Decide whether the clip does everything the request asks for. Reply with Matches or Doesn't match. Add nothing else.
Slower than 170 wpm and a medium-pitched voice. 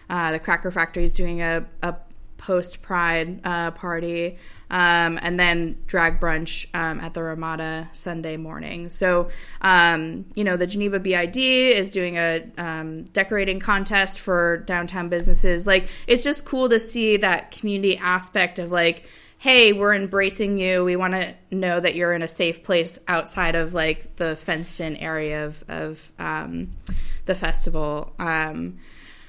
Matches